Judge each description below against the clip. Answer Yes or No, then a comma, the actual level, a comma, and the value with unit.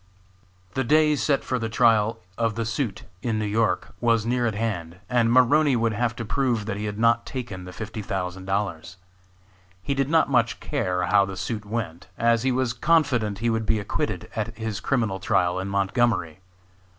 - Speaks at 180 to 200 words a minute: Yes, average, 190 wpm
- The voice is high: No, low, 115 Hz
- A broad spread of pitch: No, average, 3.3 semitones